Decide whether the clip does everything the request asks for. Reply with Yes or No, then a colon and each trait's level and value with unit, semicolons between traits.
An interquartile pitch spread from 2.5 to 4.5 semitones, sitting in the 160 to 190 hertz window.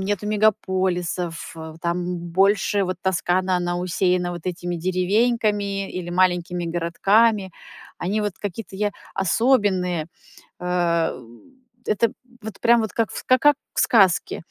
Yes: average, 2.9 semitones; medium, 185 Hz